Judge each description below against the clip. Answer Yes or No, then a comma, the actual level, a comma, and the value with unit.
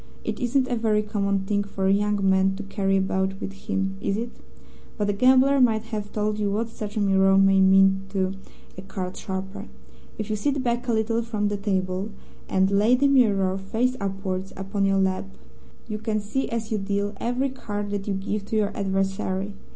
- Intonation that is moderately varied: No, narrow, 2.3 semitones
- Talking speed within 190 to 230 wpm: Yes, average, 200 wpm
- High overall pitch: Yes, high, 205 Hz